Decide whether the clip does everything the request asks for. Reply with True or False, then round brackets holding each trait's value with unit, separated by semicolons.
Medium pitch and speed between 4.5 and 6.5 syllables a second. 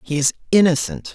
True (150 Hz; 5.8 syllables/s)